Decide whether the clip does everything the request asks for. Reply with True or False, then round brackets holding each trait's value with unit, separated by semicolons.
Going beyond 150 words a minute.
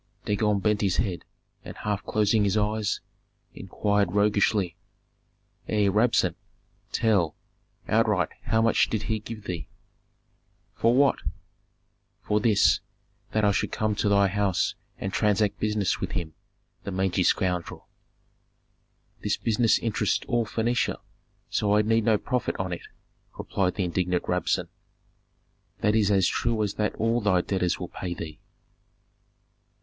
False (135 wpm)